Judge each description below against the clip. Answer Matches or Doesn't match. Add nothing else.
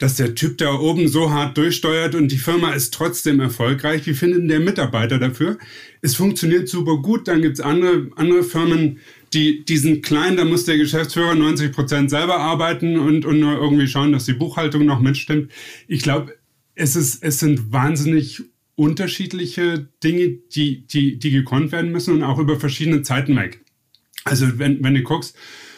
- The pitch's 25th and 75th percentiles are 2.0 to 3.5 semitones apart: Matches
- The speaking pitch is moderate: Matches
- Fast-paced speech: Doesn't match